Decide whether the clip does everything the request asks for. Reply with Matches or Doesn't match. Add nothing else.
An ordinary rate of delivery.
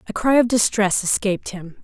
Matches